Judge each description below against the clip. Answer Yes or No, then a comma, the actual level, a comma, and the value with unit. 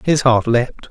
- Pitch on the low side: Yes, low, 125 Hz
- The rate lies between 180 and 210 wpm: Yes, average, 200 wpm